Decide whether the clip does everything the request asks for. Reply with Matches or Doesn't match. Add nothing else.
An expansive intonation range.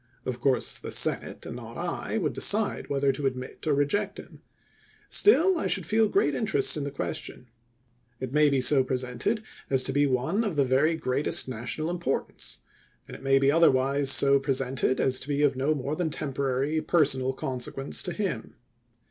Doesn't match